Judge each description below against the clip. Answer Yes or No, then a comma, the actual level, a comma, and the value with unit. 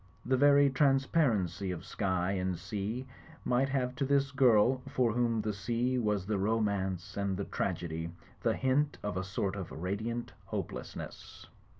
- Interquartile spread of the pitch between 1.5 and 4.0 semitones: No, average, 5.3 semitones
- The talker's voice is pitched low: Yes, low, 110 Hz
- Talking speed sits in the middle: Yes, average, 160 wpm